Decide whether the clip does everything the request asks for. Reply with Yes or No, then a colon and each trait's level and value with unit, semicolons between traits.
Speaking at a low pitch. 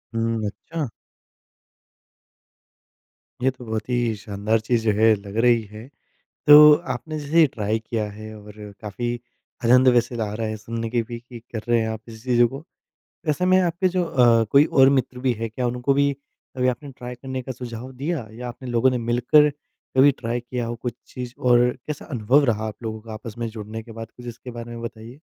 Yes: low, 120 Hz